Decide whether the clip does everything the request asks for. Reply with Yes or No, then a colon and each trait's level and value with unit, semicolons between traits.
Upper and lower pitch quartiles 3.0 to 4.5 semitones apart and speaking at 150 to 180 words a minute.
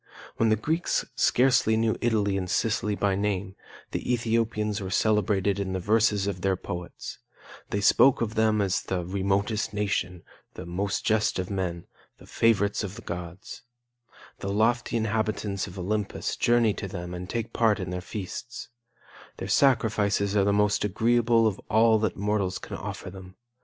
No: narrow, 2.6 semitones; average, 165 wpm